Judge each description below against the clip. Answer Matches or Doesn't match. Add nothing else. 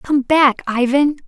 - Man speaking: Doesn't match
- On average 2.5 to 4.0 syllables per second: Matches